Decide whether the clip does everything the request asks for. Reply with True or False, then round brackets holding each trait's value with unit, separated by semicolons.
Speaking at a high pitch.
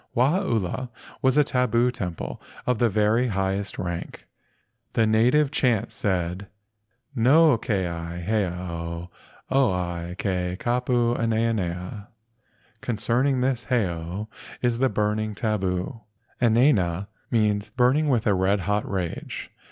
False (110 Hz)